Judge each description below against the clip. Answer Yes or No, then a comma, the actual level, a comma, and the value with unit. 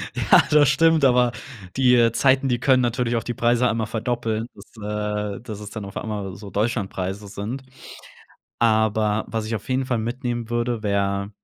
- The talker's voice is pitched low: Yes, low, 115 Hz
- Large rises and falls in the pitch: No, average, 2.7 semitones